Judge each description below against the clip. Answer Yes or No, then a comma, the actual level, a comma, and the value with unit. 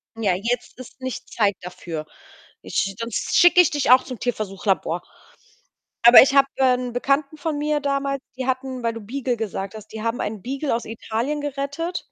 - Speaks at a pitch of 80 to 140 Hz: No, very high, 250 Hz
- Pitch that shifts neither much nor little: Yes, average, 4.2 semitones